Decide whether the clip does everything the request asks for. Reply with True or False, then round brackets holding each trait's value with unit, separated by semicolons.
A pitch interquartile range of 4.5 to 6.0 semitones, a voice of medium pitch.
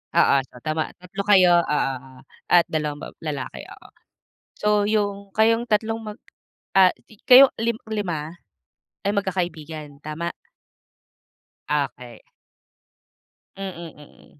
True (5.2 semitones; 180 Hz)